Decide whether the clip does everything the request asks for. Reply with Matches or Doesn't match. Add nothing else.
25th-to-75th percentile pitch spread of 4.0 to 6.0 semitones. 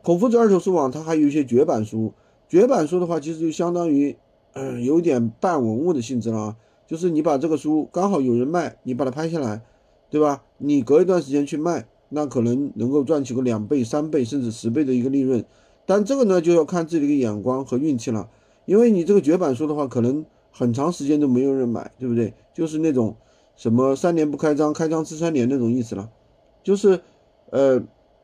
Matches